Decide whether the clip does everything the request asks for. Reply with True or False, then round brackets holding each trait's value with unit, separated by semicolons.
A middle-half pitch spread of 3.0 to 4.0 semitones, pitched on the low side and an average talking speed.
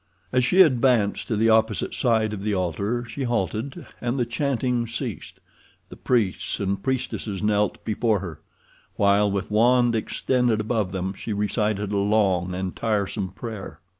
True (3.3 semitones; 110 Hz; 155 wpm)